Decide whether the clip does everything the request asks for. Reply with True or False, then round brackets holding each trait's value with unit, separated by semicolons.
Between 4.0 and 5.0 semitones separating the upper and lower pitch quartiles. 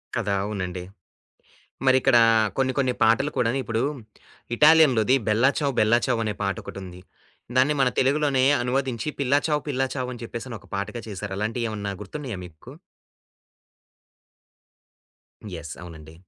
True (4.4 semitones)